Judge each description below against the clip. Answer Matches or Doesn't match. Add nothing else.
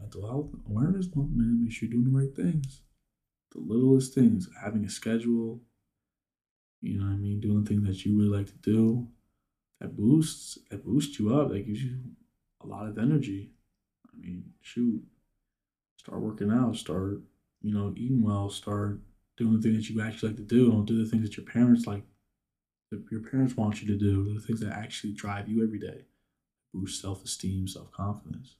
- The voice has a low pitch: Matches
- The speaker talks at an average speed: Matches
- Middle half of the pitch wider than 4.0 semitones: Doesn't match